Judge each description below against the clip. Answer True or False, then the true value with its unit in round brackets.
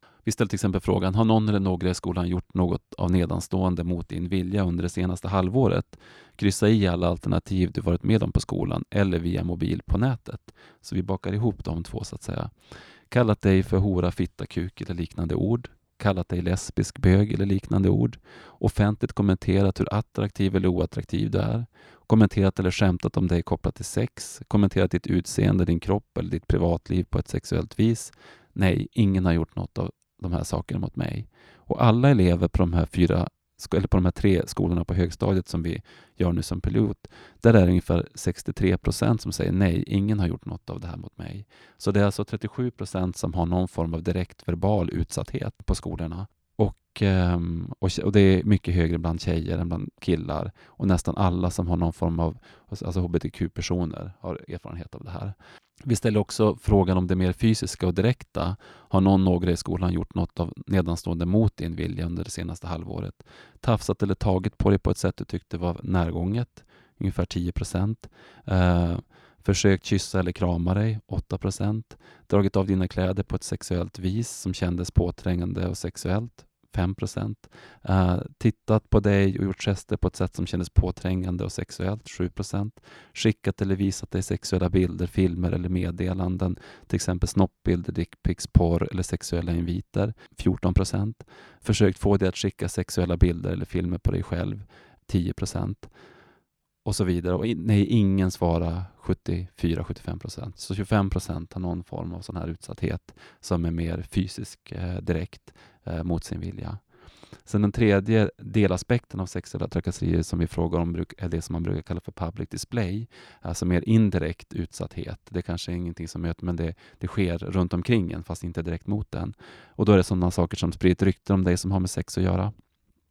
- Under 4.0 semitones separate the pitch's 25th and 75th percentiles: True (2.8 semitones)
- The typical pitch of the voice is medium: False (95 Hz)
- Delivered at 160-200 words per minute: True (180 wpm)